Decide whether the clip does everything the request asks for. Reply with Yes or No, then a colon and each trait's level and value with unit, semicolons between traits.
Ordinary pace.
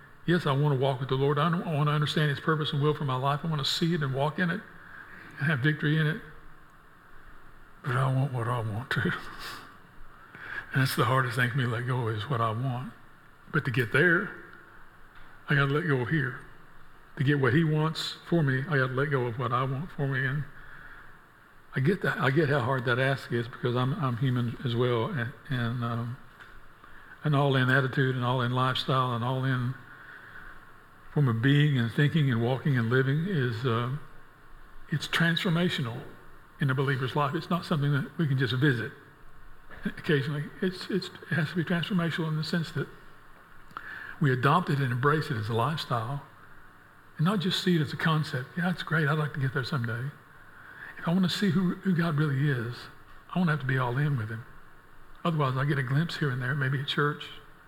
No: fast, 215 wpm